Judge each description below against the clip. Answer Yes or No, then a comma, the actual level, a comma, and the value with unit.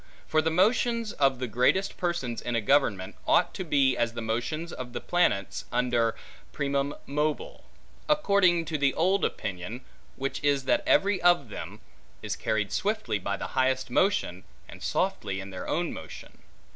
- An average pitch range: No, wide, 7.0 semitones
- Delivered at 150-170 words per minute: Yes, average, 165 wpm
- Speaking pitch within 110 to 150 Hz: Yes, medium, 140 Hz